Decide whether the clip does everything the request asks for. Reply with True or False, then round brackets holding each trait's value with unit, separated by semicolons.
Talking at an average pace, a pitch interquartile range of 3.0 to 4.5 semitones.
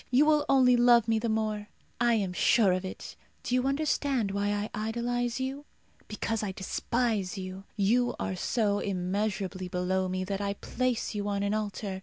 True (180 wpm; 3.7 semitones)